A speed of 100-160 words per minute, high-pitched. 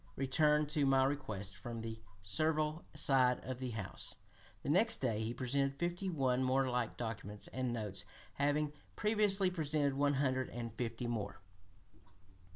No: average, 150 wpm; low, 130 Hz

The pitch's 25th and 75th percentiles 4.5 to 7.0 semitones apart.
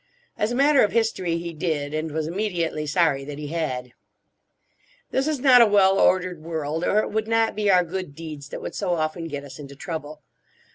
Yes: average, 5.2 semitones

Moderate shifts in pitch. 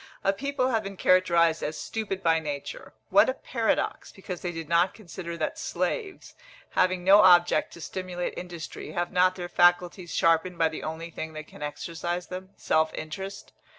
No: narrow, 2.3 semitones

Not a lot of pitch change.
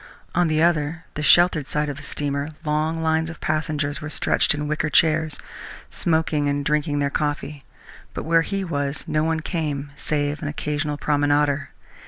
Yes: narrow, 1.6 semitones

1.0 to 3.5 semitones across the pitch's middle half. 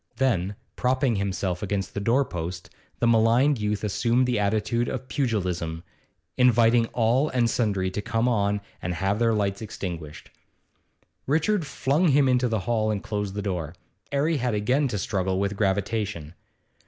No: average, 4.1 semitones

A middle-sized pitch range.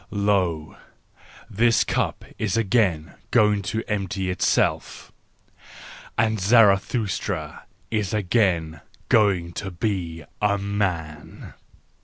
Yes: average, 3.3 semitones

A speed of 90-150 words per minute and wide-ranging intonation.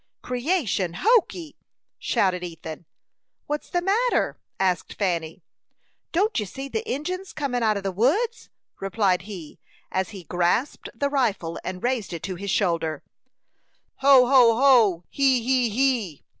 Yes: average, 140 wpm; wide, 7.2 semitones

